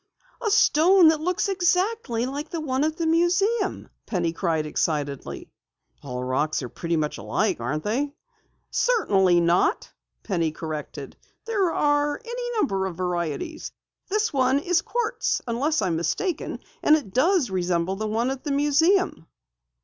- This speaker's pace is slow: No, average, 145 wpm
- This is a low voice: No, very high, 270 Hz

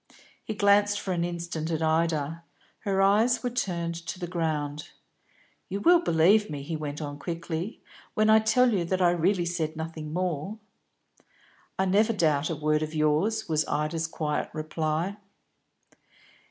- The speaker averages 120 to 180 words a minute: Yes, average, 155 wpm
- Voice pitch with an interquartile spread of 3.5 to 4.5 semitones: Yes, average, 4.2 semitones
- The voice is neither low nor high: Yes, medium, 170 Hz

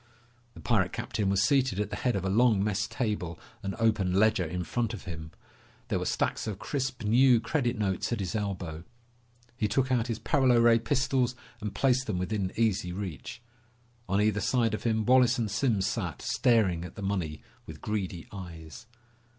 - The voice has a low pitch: Yes, low, 105 Hz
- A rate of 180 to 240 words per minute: Yes, average, 185 wpm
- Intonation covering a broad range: No, average, 3.9 semitones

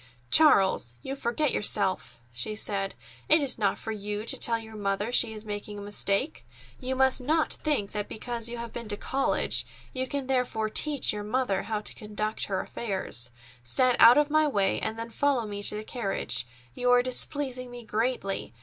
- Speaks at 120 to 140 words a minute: No, average, 190 wpm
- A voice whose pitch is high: Yes, high, 225 Hz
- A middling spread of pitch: Yes, average, 3.8 semitones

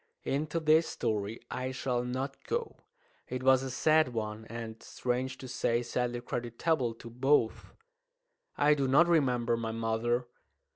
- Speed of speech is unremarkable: Yes, average, 145 wpm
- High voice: No, low, 125 Hz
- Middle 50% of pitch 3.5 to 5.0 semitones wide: No, average, 2.7 semitones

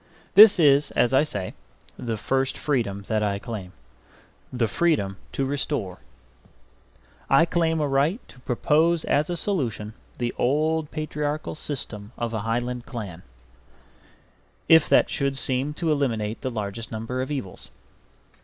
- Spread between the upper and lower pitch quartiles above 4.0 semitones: Yes, average, 5.0 semitones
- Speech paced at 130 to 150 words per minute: Yes, average, 140 wpm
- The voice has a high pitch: No, low, 130 Hz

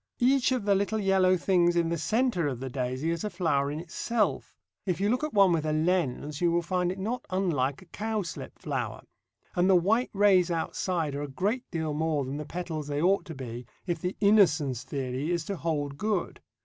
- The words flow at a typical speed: No, fast, 215 wpm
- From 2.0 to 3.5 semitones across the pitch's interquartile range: No, average, 4.8 semitones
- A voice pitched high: No, medium, 175 Hz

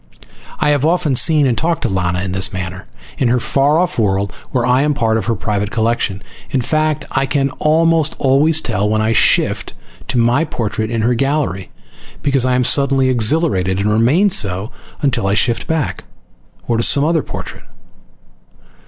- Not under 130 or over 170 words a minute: No, average, 180 wpm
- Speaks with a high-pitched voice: No, low, 125 Hz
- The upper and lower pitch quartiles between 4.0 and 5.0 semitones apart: No, wide, 5.6 semitones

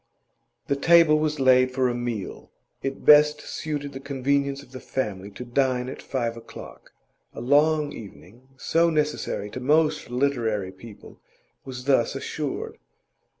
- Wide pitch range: No, average, 3.5 semitones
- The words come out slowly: No, average, 145 wpm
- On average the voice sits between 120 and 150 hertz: Yes, low, 135 Hz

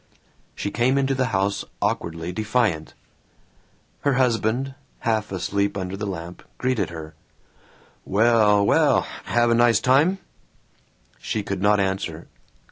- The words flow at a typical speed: No, slow, 120 wpm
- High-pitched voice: No, low, 105 Hz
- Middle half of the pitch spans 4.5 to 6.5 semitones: No, average, 4.0 semitones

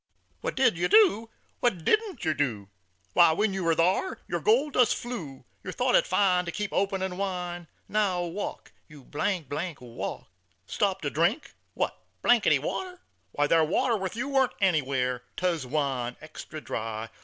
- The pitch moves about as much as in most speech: No, wide, 6.4 semitones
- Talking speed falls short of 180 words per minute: Yes, average, 155 wpm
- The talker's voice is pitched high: No, medium, 180 Hz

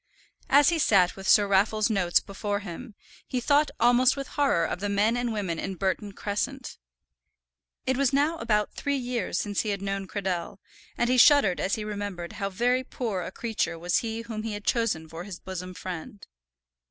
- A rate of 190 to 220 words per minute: Yes, average, 195 wpm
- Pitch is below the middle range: No, high, 210 Hz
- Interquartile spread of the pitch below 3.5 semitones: No, average, 4.2 semitones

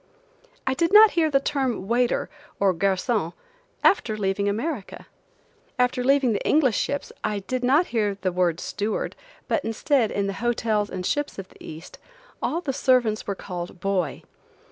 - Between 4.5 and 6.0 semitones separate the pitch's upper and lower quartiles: Yes, average, 5.2 semitones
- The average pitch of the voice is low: No, high, 225 Hz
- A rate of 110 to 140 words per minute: No, average, 165 wpm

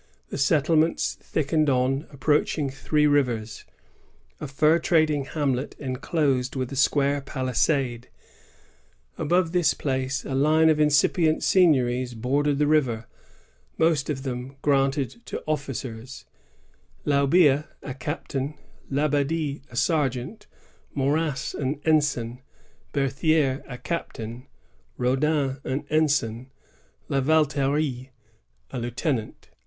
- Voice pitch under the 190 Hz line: Yes, medium, 140 Hz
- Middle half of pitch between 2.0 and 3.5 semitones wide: Yes, average, 2.8 semitones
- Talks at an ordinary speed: No, slow, 110 wpm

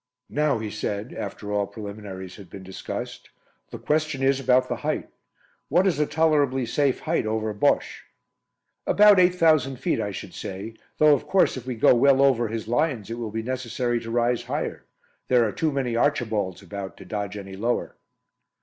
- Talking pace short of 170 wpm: No, average, 180 wpm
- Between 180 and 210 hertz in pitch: No, low, 120 Hz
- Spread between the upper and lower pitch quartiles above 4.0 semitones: Yes, average, 5.0 semitones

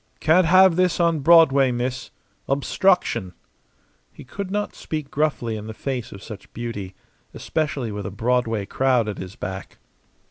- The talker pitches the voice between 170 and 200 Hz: No, low, 130 Hz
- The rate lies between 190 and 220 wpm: No, average, 150 wpm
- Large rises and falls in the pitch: Yes, wide, 6.6 semitones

